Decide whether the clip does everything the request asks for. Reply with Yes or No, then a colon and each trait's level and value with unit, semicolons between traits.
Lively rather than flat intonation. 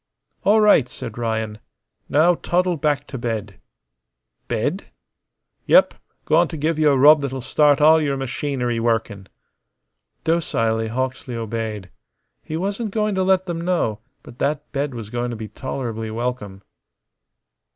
Yes: wide, 5.8 semitones